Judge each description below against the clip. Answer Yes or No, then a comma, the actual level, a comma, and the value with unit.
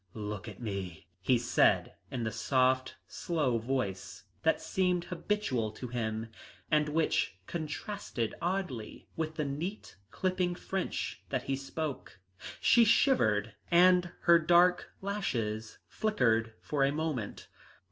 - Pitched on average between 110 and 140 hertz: Yes, low, 135 Hz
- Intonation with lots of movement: Yes, wide, 7.7 semitones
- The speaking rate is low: Yes, slow, 125 wpm